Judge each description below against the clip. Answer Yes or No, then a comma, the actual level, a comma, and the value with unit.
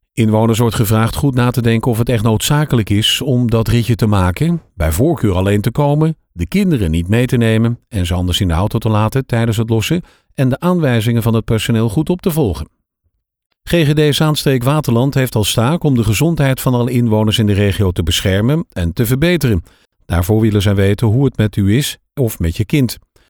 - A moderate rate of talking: No, fast, 210 wpm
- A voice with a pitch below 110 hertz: No, low, 115 Hz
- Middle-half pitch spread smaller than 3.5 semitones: No, average, 4.3 semitones